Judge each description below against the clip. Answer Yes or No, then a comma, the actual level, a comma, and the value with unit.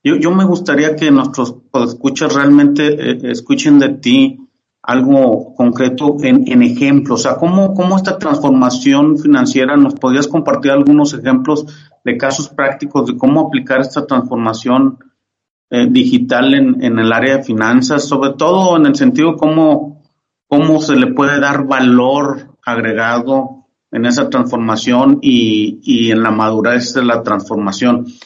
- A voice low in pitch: No, medium, 145 Hz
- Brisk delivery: No, average, 150 wpm